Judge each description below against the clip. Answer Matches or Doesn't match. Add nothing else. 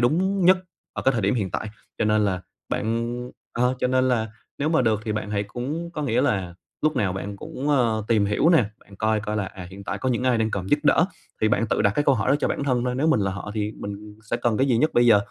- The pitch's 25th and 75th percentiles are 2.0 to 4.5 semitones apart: Matches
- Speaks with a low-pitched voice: Matches